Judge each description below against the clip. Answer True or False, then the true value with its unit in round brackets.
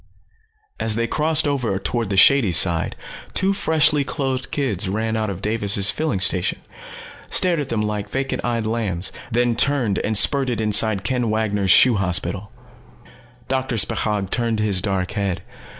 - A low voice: True (110 Hz)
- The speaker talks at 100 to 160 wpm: True (150 wpm)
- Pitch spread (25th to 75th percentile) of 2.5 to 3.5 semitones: False (4.7 semitones)